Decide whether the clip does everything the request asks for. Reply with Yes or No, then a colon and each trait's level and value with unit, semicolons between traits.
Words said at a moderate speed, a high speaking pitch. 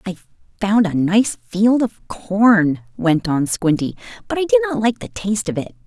Yes: average, 195 wpm; high, 210 Hz